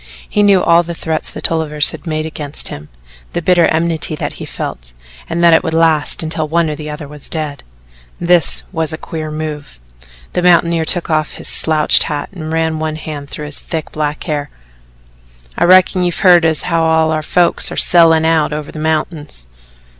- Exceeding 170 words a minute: Yes, average, 195 wpm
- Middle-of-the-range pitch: Yes, medium, 160 Hz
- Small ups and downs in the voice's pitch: Yes, narrow, 1.7 semitones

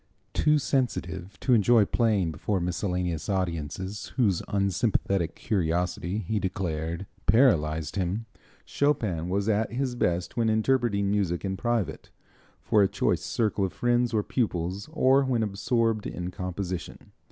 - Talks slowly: Yes, slow, 130 wpm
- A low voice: Yes, low, 100 Hz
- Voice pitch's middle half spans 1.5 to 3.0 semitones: No, average, 4.4 semitones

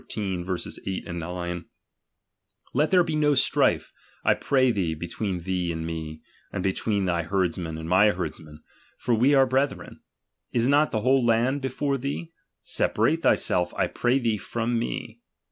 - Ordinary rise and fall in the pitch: No, wide, 7.0 semitones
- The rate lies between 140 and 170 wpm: Yes, average, 155 wpm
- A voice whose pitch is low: Yes, low, 105 Hz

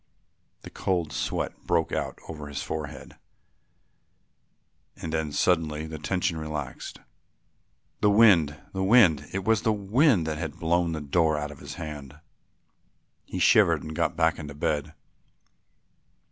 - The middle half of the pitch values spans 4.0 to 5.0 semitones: No, average, 3.3 semitones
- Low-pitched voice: Yes, very low, 80 Hz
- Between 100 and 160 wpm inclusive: Yes, average, 140 wpm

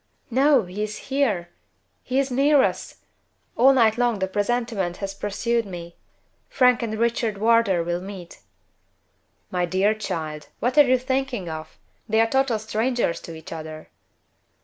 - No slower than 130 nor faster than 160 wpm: Yes, average, 150 wpm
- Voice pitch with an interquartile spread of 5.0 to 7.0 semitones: Yes, wide, 5.5 semitones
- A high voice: Yes, high, 220 Hz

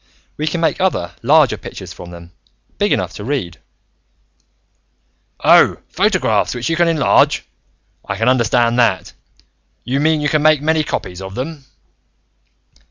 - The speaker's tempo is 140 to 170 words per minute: Yes, average, 155 wpm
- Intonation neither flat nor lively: No, wide, 7.7 semitones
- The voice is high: No, low, 130 Hz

